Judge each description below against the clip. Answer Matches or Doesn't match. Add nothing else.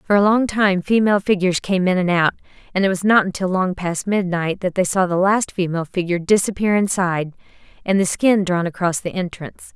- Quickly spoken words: Matches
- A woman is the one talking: Matches